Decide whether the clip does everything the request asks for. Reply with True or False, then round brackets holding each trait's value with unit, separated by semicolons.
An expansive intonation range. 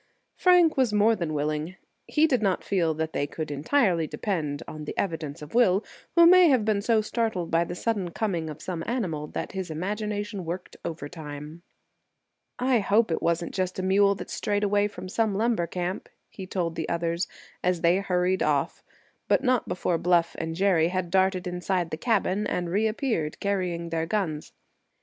False (4.0 semitones)